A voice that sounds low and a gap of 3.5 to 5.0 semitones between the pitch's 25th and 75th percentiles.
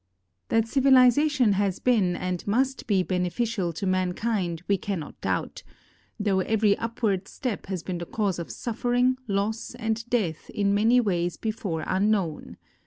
No: high, 205 Hz; average, 4.0 semitones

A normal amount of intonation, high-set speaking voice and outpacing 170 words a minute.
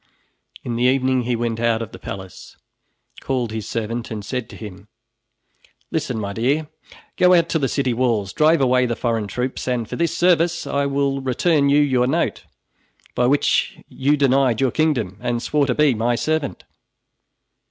No: average, 3.6 semitones; low, 125 Hz; average, 180 wpm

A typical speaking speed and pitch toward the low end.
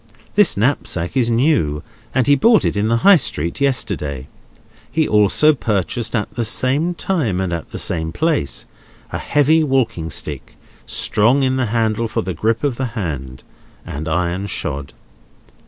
Yes: average, 160 wpm; low, 115 Hz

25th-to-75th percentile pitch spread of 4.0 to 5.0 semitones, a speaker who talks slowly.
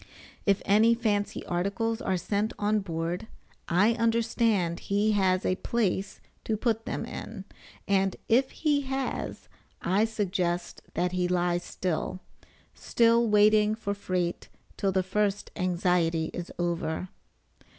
No: average, 3.6 semitones; slow, 130 wpm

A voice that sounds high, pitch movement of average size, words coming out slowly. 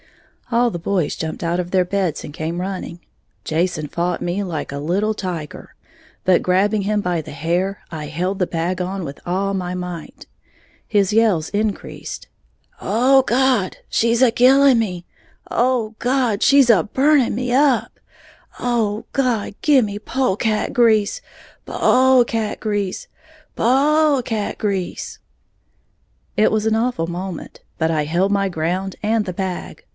No: high, 200 Hz; average, 4.7 semitones; average, 150 wpm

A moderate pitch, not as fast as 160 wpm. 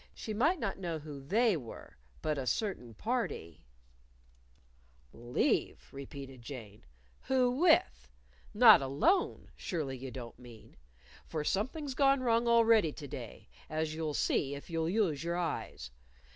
Yes: medium, 160 Hz; slow, 135 wpm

